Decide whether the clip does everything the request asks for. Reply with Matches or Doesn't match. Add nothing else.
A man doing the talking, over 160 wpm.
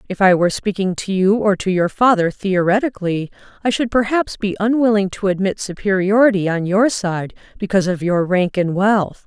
Doesn't match